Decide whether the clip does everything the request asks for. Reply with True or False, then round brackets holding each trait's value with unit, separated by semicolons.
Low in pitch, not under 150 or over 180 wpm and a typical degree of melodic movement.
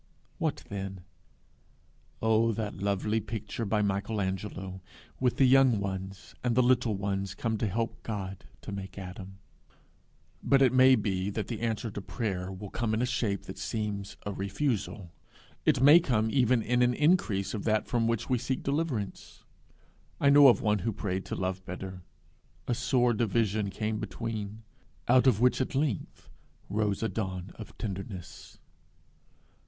True (110 Hz; 160 wpm; 3.7 semitones)